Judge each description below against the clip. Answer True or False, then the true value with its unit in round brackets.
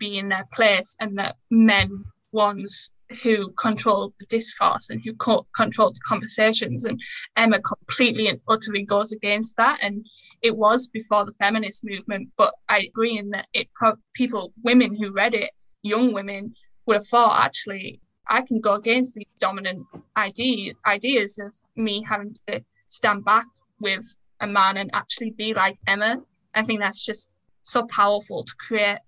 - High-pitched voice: True (215 Hz)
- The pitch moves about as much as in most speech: False (2.1 semitones)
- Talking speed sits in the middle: True (165 wpm)